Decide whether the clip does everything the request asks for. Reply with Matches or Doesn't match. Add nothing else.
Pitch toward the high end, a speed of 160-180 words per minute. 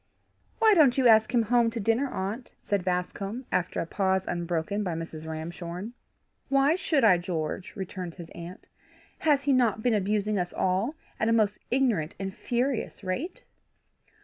Matches